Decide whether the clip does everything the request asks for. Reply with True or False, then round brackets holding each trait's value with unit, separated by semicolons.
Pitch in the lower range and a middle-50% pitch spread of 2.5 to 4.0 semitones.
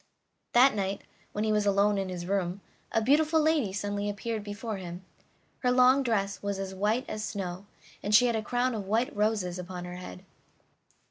False (205 Hz; 3.2 semitones)